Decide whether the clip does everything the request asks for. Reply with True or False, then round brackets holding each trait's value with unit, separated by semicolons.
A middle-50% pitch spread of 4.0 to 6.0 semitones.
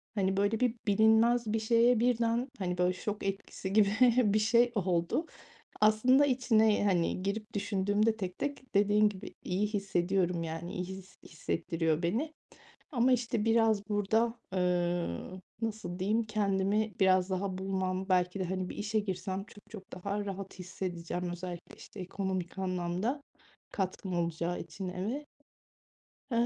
False (3.1 semitones)